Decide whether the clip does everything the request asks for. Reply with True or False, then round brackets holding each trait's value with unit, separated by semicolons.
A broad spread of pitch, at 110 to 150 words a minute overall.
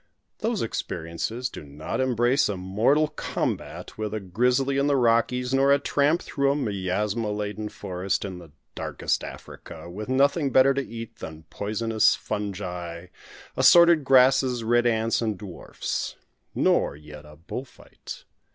True (5.9 semitones; 140 wpm)